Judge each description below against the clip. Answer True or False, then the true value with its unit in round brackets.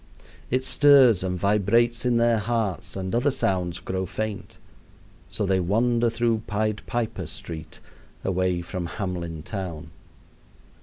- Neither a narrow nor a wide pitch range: True (4.3 semitones)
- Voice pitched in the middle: False (100 Hz)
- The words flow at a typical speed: False (125 wpm)